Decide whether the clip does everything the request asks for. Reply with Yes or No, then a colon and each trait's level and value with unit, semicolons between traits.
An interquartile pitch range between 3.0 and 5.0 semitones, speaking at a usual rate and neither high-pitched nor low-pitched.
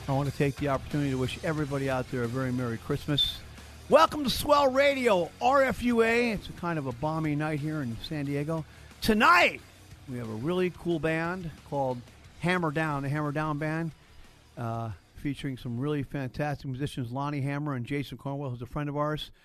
Yes: average, 3.8 semitones; average, 190 wpm; medium, 145 Hz